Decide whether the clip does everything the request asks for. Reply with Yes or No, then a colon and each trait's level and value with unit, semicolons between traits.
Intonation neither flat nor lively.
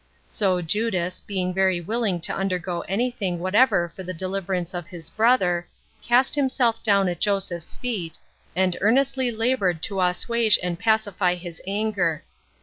Yes: average, 3.8 semitones